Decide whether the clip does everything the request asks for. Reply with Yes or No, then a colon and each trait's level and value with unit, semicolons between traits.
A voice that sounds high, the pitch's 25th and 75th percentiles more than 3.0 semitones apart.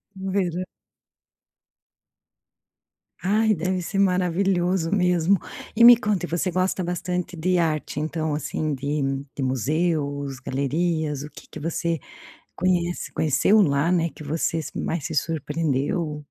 No: medium, 165 Hz; average, 3.5 semitones